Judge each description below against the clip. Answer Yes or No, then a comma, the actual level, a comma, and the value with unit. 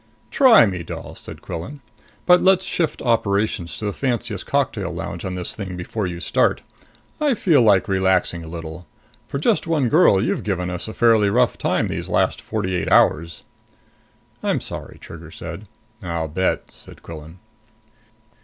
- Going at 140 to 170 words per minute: Yes, average, 165 wpm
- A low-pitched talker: Yes, very low, 95 Hz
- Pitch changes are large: Yes, wide, 5.9 semitones